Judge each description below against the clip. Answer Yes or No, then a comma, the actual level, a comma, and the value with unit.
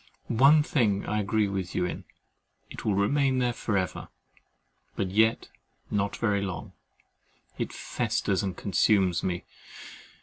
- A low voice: Yes, low, 100 Hz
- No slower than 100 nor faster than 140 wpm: Yes, slow, 135 wpm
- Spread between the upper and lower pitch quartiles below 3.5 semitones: Yes, average, 2.8 semitones